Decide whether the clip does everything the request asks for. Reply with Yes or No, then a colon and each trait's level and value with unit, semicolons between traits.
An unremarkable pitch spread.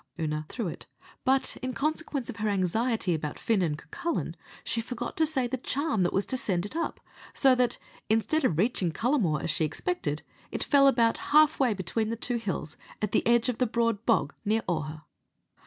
No: wide, 5.8 semitones